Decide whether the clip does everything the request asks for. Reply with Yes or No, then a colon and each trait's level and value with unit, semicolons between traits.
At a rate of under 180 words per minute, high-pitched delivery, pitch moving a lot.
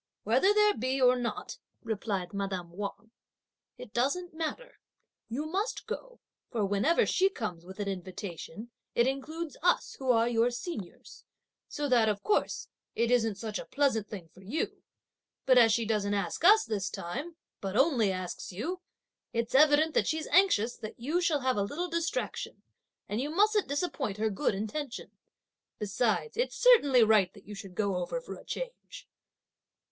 Yes: average, 165 wpm; high, 240 Hz; wide, 7.4 semitones